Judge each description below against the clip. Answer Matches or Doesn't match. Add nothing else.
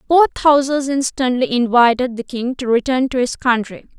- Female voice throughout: Matches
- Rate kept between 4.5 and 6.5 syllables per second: Matches